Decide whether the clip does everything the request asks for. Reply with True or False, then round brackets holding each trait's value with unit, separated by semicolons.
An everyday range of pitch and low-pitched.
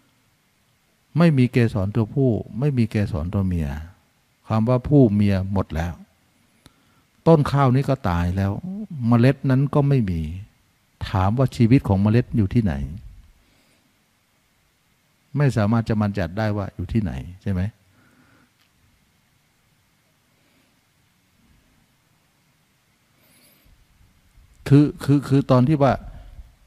False (5.7 semitones; 115 Hz)